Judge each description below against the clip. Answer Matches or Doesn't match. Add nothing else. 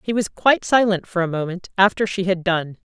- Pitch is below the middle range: Doesn't match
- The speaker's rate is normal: Doesn't match